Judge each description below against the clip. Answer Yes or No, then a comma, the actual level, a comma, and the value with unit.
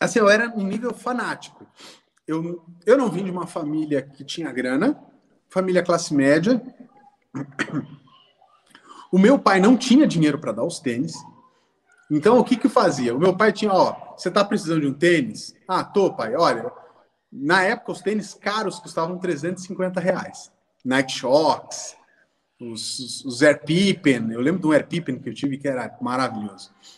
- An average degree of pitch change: No, wide, 6.5 semitones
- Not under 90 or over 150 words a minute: No, average, 170 wpm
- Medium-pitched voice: Yes, medium, 180 Hz